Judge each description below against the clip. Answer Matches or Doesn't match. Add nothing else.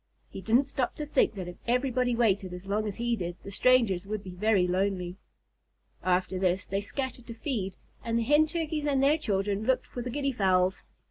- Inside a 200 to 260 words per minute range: Matches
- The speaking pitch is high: Matches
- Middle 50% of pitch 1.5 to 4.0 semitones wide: Doesn't match